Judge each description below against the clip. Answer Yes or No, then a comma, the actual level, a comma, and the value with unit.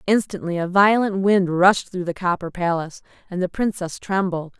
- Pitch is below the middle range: No, medium, 185 Hz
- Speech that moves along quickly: No, average, 170 wpm